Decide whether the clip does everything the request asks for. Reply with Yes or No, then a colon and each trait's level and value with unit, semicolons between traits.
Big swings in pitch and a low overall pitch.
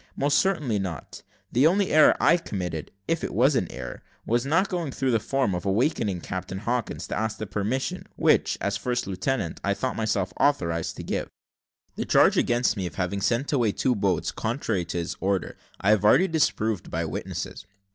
Yes: wide, 5.9 semitones; low, 110 Hz